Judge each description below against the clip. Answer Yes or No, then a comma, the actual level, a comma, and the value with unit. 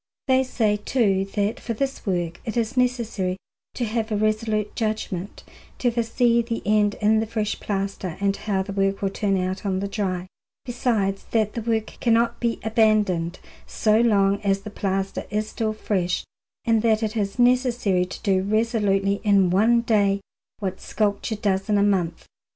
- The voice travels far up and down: No, narrow, 2.6 semitones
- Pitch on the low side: No, high, 210 Hz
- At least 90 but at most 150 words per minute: No, average, 175 wpm